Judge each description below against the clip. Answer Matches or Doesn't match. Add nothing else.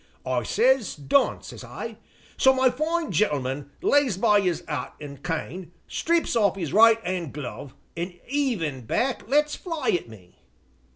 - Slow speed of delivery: Doesn't match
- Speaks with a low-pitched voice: Doesn't match